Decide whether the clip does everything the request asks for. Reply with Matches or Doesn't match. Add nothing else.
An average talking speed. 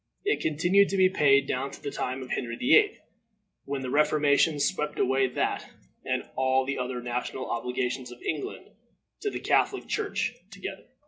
Matches